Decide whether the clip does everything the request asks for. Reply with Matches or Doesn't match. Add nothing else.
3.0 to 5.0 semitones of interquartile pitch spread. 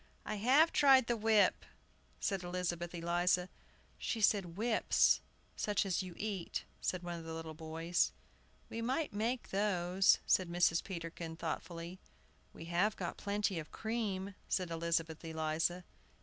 Matches